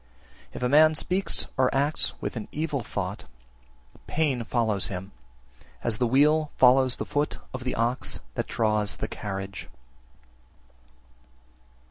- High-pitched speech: No, low, 125 Hz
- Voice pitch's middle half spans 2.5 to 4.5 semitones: No, average, 5.3 semitones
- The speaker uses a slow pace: Yes, slow, 130 wpm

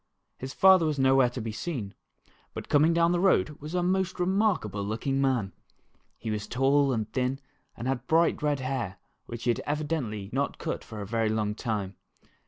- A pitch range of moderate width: No, wide, 5.8 semitones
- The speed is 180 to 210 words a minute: Yes, average, 190 wpm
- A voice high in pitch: No, low, 135 Hz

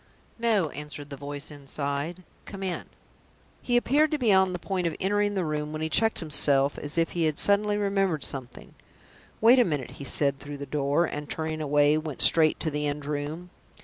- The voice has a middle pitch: Yes, medium, 155 Hz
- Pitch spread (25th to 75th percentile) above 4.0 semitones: Yes, average, 4.8 semitones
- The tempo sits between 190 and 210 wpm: Yes, average, 200 wpm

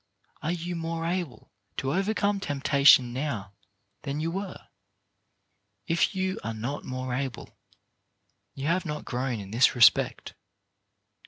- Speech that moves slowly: Yes, slow, 130 wpm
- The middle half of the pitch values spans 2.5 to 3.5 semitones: No, average, 5.3 semitones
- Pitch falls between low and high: Yes, medium, 145 Hz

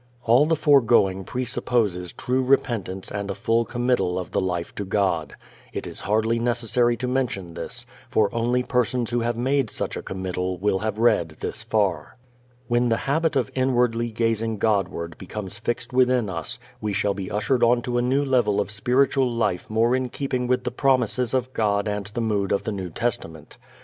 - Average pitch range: Yes, average, 3.8 semitones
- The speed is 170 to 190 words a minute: Yes, average, 185 wpm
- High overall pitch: No, low, 115 Hz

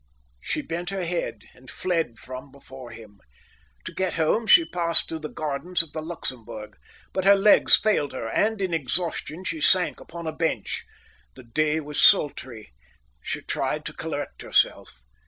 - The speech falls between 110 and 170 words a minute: Yes, average, 165 wpm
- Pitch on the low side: No, medium, 160 Hz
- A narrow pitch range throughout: No, wide, 5.5 semitones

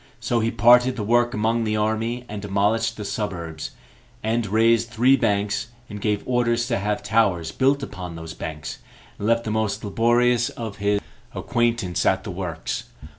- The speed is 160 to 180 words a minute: Yes, average, 170 wpm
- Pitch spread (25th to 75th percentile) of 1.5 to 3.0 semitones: Yes, narrow, 2.6 semitones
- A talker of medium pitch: No, low, 110 Hz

